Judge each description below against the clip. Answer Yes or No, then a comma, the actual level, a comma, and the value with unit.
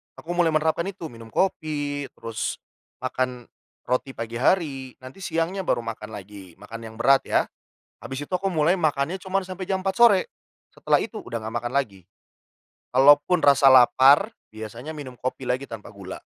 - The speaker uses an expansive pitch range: Yes, wide, 6.2 semitones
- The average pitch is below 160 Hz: Yes, medium, 140 Hz